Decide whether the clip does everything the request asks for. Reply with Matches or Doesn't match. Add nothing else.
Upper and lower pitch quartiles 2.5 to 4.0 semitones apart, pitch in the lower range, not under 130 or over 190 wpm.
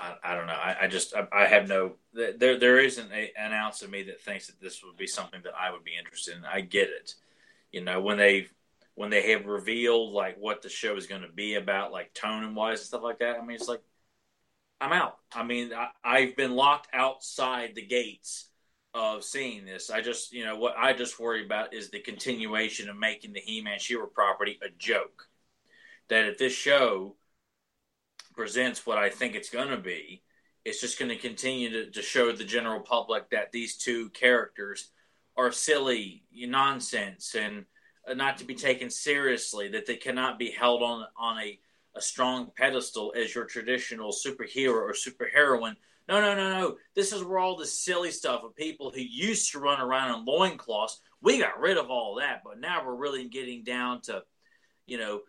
Doesn't match